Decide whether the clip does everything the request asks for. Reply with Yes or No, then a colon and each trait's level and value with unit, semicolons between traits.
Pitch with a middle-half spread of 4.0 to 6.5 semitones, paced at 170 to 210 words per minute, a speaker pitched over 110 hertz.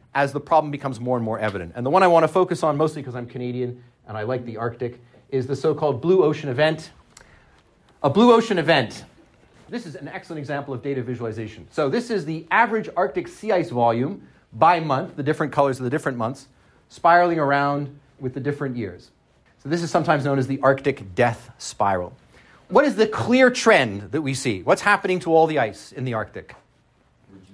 Yes: average, 4.8 semitones; fast, 205 wpm; medium, 140 Hz